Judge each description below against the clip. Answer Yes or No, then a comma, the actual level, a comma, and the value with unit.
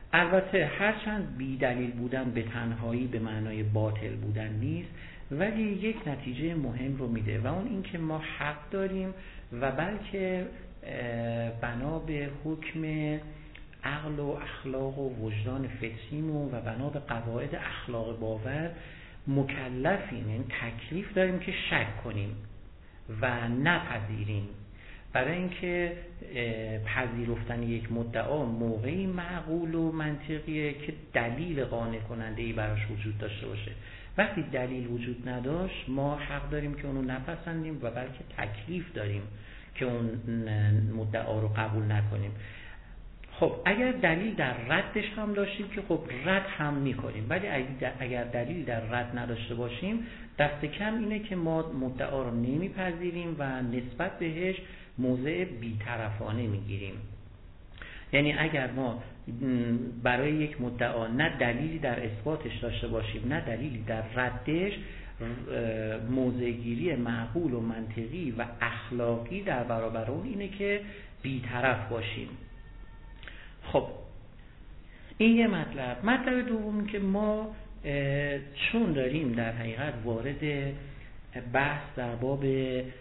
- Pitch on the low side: Yes, low, 125 Hz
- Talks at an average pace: Yes, average, 120 wpm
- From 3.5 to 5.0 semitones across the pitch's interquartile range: No, wide, 5.4 semitones